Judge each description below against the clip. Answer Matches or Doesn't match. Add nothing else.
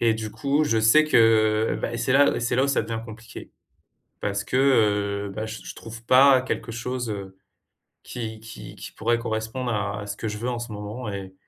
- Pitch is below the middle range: Matches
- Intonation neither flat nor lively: Doesn't match